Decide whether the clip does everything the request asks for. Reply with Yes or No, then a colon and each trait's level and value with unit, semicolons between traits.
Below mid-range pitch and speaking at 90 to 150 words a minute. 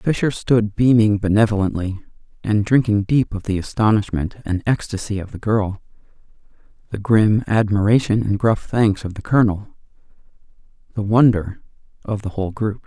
Yes: low, 105 Hz; average, 140 wpm